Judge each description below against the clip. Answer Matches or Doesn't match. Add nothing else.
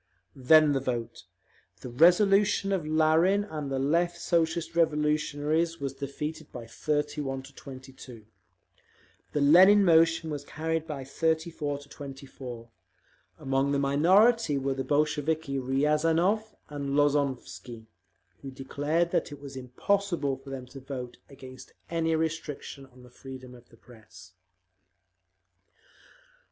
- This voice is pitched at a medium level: Matches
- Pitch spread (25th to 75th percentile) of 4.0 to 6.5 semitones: Doesn't match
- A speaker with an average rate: Doesn't match